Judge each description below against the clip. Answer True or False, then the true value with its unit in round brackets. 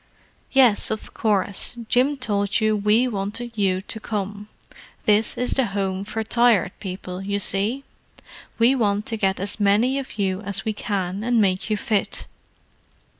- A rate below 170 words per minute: True (160 wpm)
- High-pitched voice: True (210 Hz)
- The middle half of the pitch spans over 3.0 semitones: False (2.6 semitones)